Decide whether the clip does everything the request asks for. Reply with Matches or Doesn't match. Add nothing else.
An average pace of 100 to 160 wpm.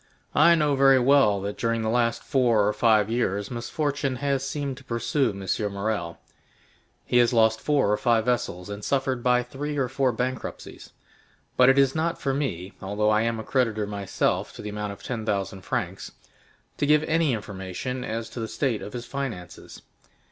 Doesn't match